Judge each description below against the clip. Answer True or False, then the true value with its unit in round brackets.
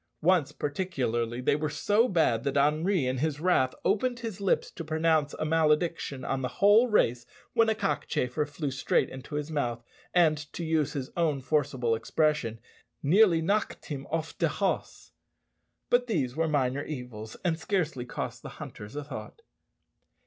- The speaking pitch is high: False (150 Hz)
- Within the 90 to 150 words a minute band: False (165 wpm)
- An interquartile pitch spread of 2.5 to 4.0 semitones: False (4.8 semitones)